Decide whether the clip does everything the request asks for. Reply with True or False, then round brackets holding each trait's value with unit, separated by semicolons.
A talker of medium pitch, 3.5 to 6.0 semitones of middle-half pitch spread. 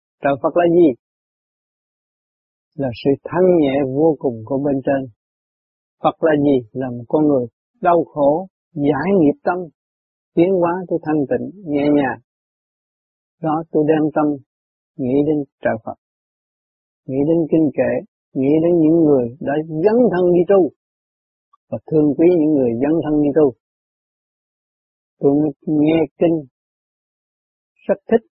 False (150 Hz; 3.1 semitones)